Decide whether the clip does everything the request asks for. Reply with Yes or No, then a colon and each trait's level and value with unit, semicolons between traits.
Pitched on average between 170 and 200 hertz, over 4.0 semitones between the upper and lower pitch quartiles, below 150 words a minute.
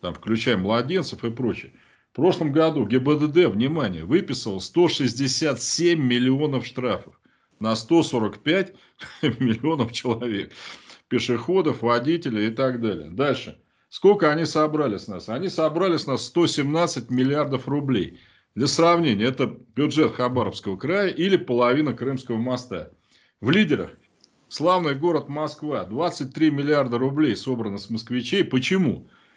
No: low, 135 Hz; average, 4.6 semitones; average, 120 wpm